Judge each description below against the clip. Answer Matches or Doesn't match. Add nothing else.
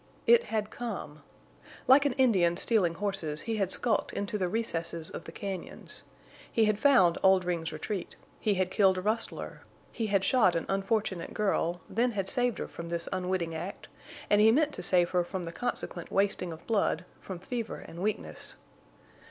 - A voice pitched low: Doesn't match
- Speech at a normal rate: Matches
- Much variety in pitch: Doesn't match